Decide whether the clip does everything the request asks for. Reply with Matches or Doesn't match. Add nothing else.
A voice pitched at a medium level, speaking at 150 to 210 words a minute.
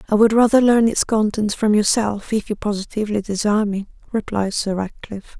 Doesn't match